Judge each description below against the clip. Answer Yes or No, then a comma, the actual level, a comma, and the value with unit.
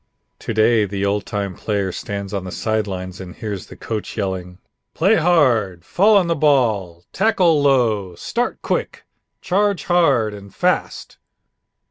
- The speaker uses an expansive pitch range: Yes, wide, 7.8 semitones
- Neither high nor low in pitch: No, low, 110 Hz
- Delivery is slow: No, average, 150 wpm